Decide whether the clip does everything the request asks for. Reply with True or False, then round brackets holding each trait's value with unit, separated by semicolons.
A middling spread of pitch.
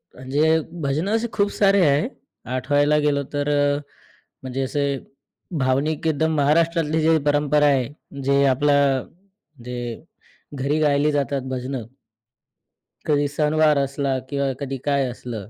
False (1.8 semitones)